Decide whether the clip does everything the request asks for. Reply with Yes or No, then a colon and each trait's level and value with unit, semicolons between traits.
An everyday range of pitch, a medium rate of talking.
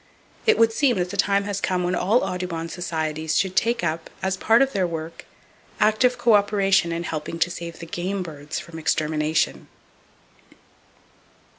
Yes: average, 3.7 semitones; average, 170 wpm